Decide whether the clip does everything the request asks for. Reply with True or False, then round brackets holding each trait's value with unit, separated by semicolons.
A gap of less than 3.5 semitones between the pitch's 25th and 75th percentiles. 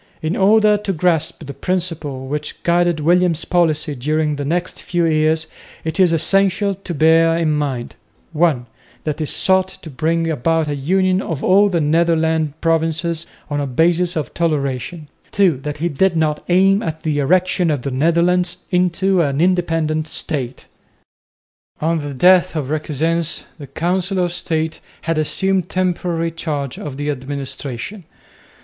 True (3.0 semitones)